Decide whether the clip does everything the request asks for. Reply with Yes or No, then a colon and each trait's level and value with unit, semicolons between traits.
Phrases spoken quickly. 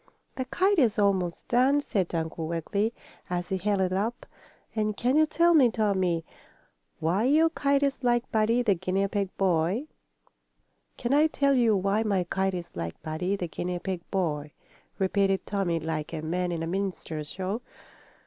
No: average, 170 wpm